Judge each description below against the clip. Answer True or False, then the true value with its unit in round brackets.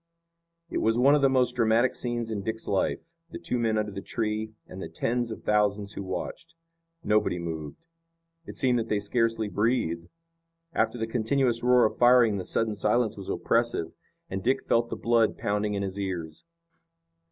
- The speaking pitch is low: True (110 Hz)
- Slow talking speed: False (180 wpm)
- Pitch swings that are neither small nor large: True (3.0 semitones)